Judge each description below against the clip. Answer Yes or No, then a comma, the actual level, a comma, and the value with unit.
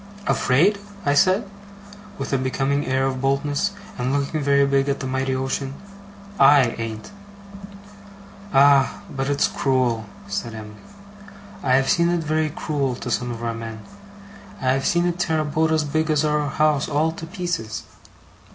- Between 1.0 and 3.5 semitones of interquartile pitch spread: Yes, average, 3.0 semitones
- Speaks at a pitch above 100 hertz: Yes, medium, 140 Hz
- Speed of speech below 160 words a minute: No, average, 165 wpm